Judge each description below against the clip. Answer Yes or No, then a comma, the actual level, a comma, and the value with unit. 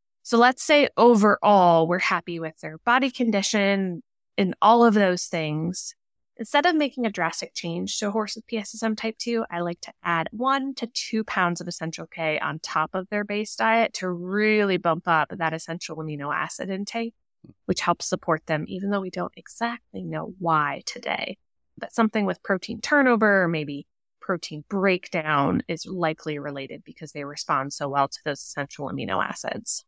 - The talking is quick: No, average, 175 wpm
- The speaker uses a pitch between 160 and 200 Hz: Yes, medium, 185 Hz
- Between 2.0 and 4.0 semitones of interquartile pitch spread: No, wide, 5.4 semitones